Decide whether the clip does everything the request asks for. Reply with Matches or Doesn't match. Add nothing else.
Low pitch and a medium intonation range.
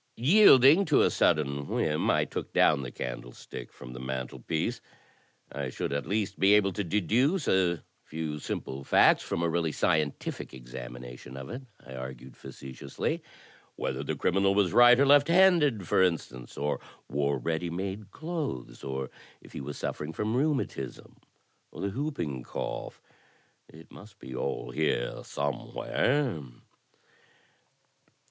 Doesn't match